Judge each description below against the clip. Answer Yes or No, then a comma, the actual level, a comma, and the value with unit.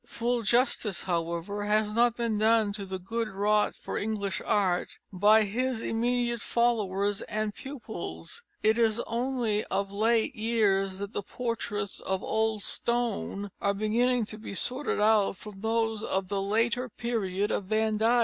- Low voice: No, high, 215 Hz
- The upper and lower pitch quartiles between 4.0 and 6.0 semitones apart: No, narrow, 2.5 semitones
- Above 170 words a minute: No, average, 155 wpm